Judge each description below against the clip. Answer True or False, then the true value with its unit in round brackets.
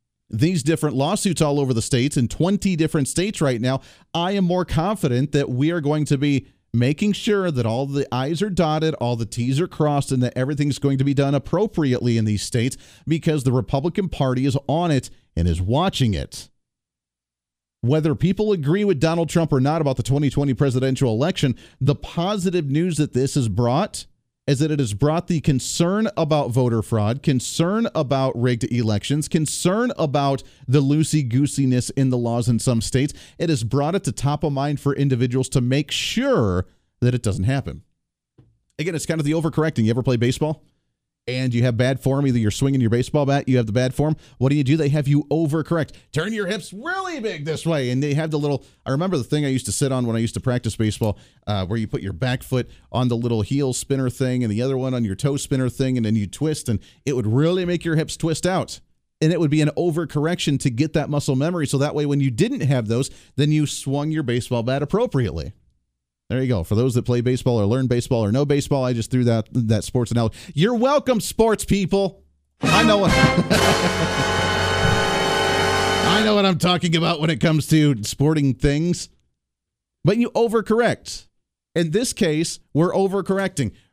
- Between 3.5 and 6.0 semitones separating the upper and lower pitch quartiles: True (4.6 semitones)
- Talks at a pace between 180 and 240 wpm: True (205 wpm)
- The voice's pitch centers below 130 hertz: False (140 Hz)